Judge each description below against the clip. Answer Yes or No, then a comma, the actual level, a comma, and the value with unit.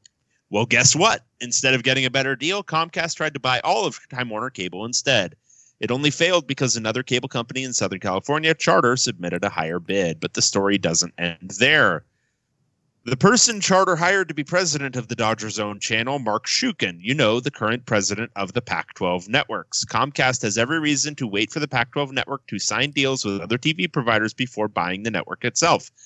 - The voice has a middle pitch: No, low, 125 Hz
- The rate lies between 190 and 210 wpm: Yes, average, 200 wpm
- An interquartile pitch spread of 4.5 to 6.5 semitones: Yes, average, 5.2 semitones